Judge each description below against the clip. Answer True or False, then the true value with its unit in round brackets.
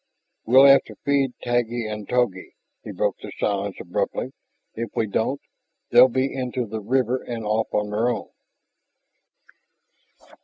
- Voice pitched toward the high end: False (120 Hz)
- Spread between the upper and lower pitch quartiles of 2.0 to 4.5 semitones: True (3.3 semitones)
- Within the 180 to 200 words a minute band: False (145 wpm)